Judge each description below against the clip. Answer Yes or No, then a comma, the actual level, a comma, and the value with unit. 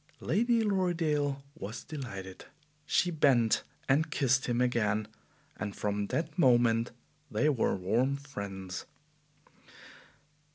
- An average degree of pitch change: No, wide, 5.9 semitones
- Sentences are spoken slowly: Yes, slow, 100 wpm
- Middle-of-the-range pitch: No, low, 125 Hz